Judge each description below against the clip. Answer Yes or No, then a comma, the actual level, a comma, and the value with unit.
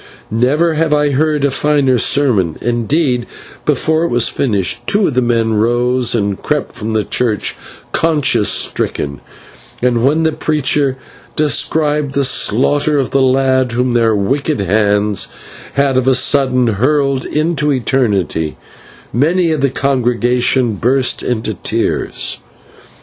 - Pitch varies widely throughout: No, average, 3.9 semitones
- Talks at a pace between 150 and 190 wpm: No, slow, 135 wpm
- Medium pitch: No, low, 130 Hz